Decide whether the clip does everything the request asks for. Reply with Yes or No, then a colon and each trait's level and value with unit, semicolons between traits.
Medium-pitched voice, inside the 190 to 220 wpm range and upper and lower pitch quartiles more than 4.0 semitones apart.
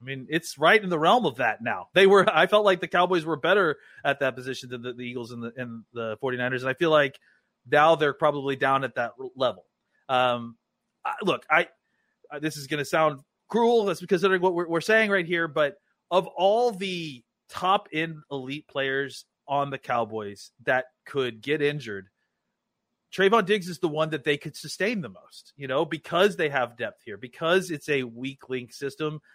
Yes: medium, 150 Hz; average, 200 wpm; average, 5.3 semitones